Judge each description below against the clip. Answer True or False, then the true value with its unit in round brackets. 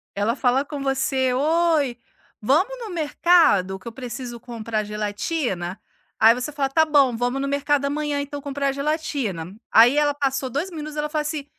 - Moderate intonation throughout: True (3.9 semitones)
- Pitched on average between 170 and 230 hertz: False (275 Hz)